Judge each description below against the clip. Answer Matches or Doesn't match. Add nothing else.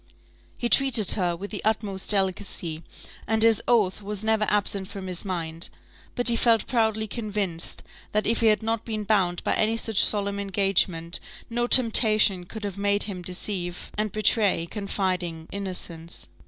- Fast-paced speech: Doesn't match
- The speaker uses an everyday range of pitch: Matches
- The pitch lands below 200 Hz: Doesn't match